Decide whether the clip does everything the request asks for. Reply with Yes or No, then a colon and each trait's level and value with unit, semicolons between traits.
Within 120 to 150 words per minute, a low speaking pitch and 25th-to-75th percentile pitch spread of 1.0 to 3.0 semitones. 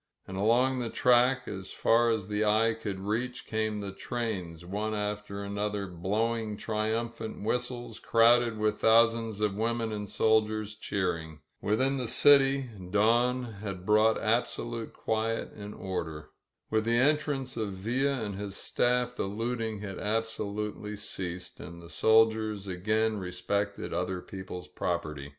Yes: average, 140 wpm; low, 110 Hz; narrow, 2.6 semitones